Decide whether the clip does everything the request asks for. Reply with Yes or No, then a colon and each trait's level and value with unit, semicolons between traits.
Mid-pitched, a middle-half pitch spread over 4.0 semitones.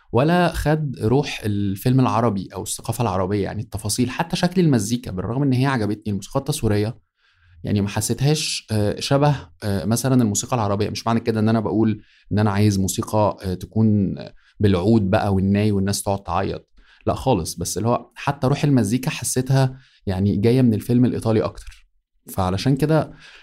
No: low, 110 Hz; average, 4.4 semitones